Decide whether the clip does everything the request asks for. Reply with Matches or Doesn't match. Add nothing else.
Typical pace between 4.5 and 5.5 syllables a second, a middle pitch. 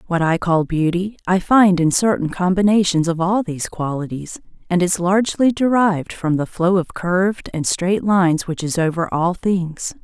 Matches